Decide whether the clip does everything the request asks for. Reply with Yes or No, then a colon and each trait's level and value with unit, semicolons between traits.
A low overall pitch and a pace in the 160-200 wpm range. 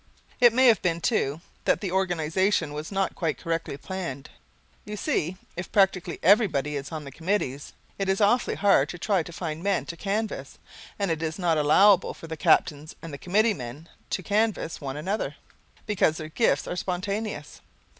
No: medium, 175 Hz; average, 180 wpm